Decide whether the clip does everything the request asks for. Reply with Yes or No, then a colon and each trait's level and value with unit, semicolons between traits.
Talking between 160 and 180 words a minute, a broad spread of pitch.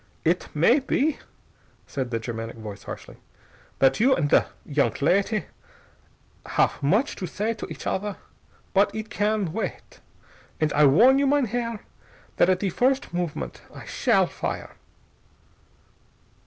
No: average, 140 wpm; wide, 7.9 semitones